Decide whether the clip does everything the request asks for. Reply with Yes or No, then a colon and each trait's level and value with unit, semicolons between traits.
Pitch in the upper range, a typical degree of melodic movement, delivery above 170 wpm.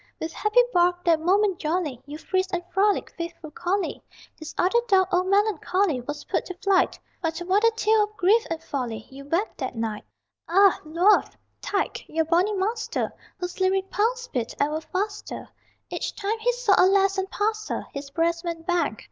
Yes: very high, 365 Hz; average, 4.0 semitones; average, 180 wpm